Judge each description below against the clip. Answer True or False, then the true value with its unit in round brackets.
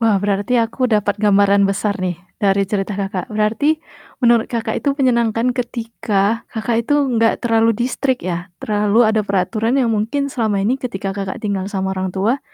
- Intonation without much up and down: False (3.0 semitones)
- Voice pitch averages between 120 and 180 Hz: False (220 Hz)